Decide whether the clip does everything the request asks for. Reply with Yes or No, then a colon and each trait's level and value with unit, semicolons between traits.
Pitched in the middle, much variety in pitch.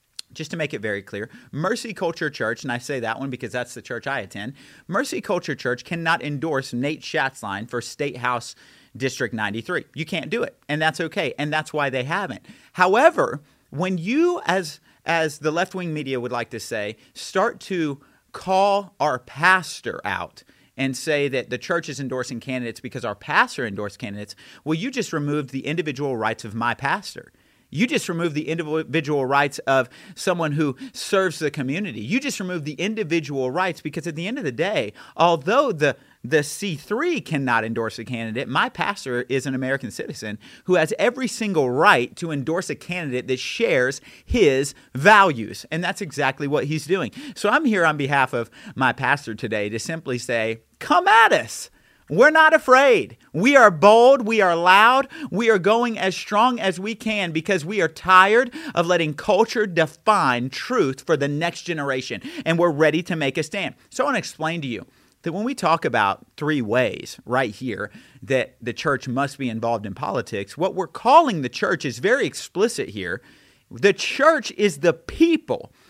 Yes: medium, 160 Hz; wide, 6.5 semitones